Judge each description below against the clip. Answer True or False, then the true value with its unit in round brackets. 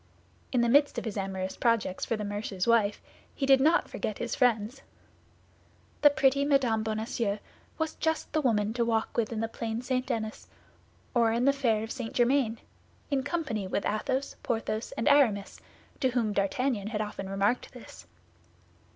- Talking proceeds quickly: False (170 wpm)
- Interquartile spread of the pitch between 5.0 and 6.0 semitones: False (3.8 semitones)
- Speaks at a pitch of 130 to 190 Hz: False (230 Hz)